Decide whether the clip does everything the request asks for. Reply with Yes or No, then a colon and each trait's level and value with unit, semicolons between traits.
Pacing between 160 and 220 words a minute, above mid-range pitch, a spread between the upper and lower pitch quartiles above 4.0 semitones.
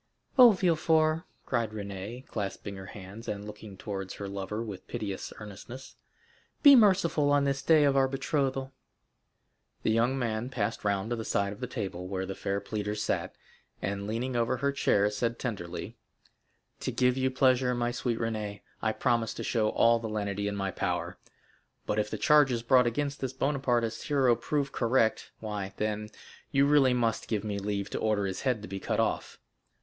No: average, 185 wpm; low, 115 Hz; average, 4.5 semitones